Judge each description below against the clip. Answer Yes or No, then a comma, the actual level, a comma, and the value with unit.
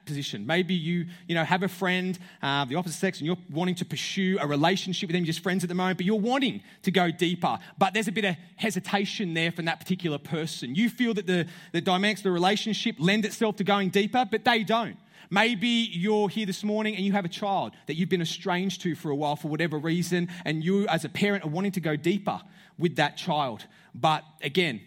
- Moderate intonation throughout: Yes, average, 3.1 semitones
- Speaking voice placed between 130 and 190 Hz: Yes, medium, 185 Hz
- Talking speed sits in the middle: No, fast, 230 wpm